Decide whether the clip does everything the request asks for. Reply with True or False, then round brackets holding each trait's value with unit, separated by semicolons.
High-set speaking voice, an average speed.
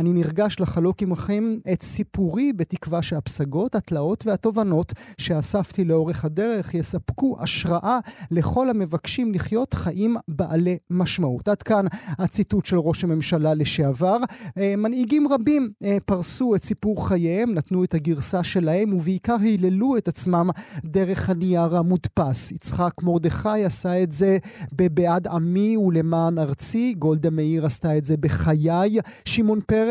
False (180 Hz; 125 wpm)